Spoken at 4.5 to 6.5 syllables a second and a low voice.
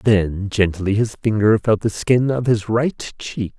No: 3.8 syllables/s; low, 110 Hz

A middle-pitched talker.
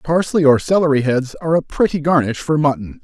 Yes: medium, 145 Hz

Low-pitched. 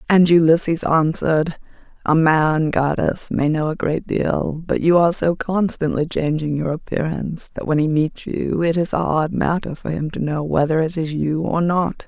No: medium, 160 Hz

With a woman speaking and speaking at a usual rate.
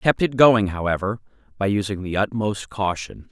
No: male; average, 180 wpm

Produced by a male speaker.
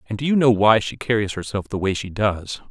Yes: male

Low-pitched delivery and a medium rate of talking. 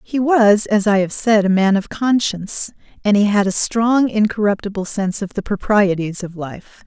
No: high, 205 Hz; average, 190 wpm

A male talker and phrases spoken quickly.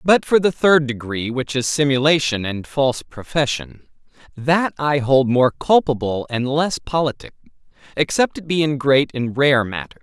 No: male; average, 160 wpm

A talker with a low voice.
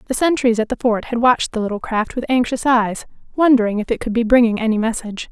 No: high, 235 Hz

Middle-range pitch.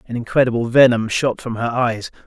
No: low, 120 Hz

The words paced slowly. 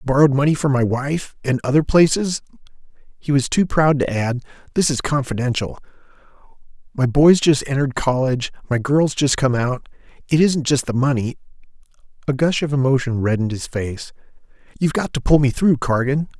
No: average, 155 wpm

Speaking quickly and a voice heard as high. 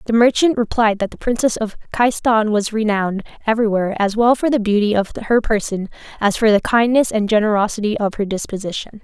No: average, 185 wpm; high, 215 Hz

